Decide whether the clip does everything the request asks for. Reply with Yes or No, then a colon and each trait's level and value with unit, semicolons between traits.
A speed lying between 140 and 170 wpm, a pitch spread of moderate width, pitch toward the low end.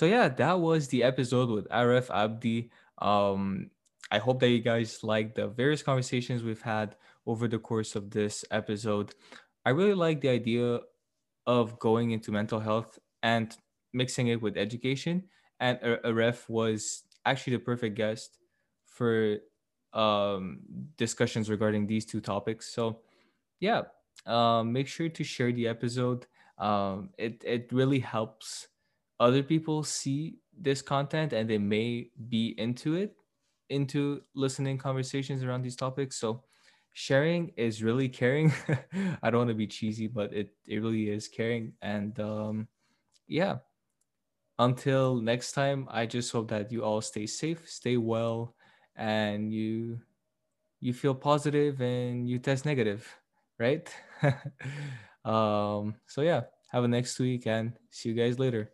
Yes: average, 145 wpm; average, 3.4 semitones; low, 120 Hz